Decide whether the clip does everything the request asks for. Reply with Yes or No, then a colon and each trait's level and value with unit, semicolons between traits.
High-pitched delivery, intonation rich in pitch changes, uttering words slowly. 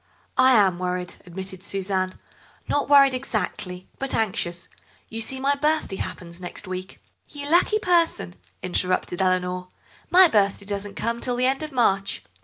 No: high, 200 Hz; wide, 6.6 semitones; average, 150 wpm